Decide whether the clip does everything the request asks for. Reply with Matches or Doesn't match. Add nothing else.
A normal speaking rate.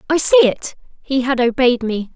Matches